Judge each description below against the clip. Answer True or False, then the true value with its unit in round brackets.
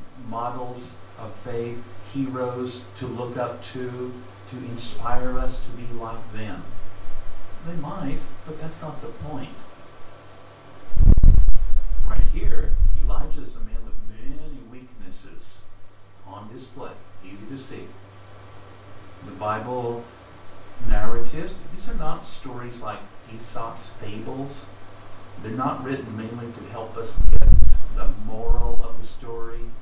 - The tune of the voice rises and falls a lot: False (4.0 semitones)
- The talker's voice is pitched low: True (110 Hz)